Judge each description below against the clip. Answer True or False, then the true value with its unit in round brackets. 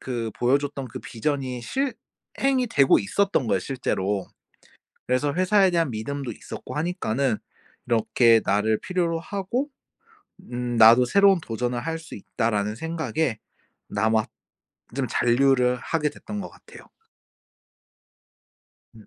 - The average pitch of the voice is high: False (130 Hz)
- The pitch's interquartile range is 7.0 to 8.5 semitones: False (6.4 semitones)